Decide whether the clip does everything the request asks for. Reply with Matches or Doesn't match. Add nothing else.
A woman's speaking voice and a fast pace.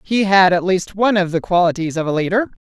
Matches